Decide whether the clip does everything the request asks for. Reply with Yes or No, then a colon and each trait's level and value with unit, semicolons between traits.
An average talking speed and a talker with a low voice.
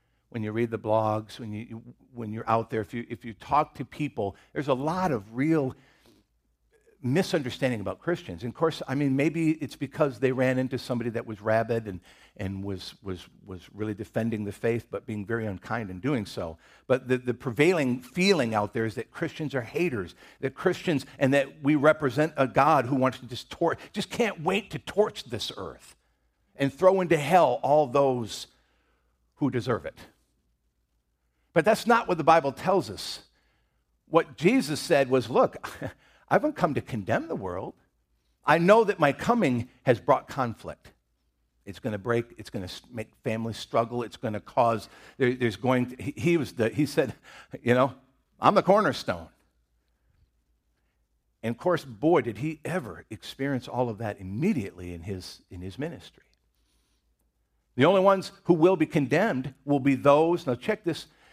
Yes: average, 180 wpm; low, 120 Hz